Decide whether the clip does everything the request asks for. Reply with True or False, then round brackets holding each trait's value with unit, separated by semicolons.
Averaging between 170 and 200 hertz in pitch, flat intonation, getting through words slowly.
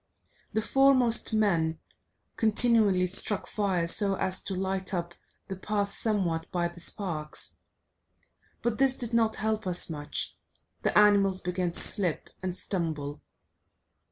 False (190 Hz; 3.9 semitones; 130 wpm)